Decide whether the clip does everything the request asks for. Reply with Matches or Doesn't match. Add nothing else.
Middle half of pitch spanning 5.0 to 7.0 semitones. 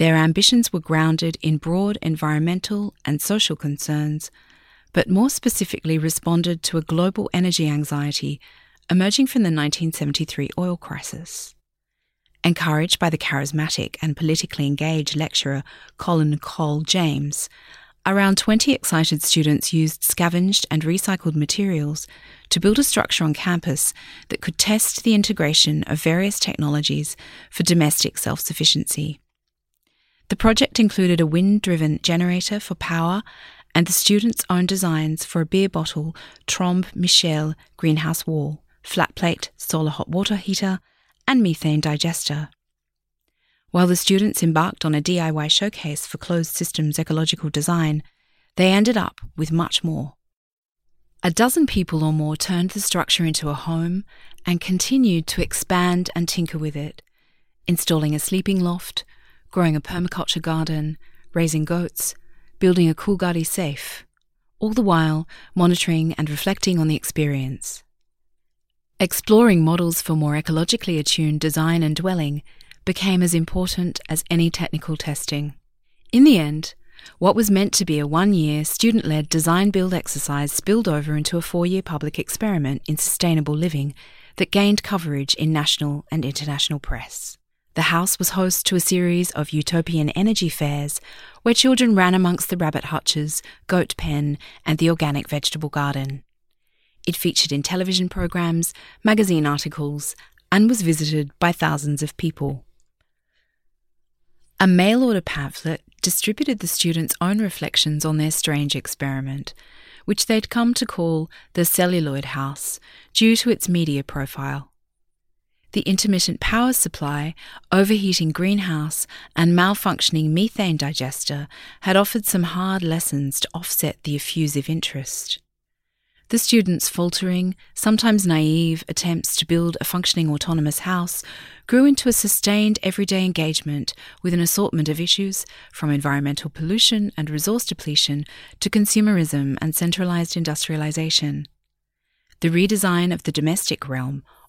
Doesn't match